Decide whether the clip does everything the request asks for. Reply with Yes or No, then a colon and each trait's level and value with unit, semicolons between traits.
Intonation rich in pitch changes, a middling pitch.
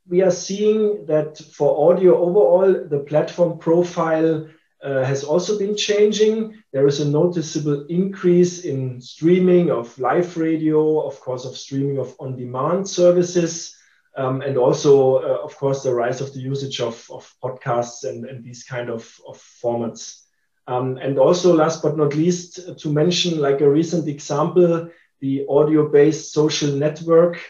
No: average, 4.4 semitones; medium, 155 Hz